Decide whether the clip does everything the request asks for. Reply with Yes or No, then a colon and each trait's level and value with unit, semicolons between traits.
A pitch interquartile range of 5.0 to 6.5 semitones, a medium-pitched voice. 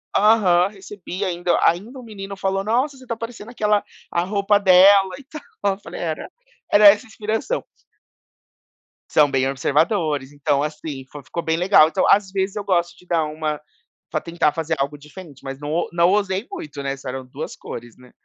Yes: average, 5.3 semitones; medium, 180 Hz